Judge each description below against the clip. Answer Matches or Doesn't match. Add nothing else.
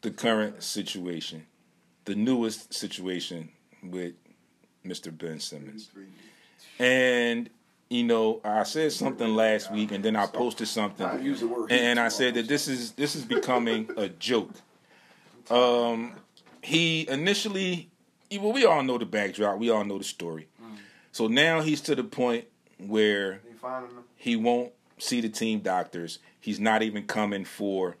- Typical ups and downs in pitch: Matches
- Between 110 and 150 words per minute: Matches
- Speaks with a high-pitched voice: Doesn't match